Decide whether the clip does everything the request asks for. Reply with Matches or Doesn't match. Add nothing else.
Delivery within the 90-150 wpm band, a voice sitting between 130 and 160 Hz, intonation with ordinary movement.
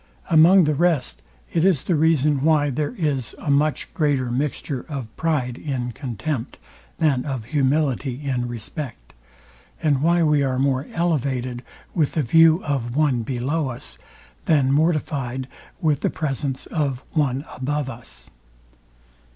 Matches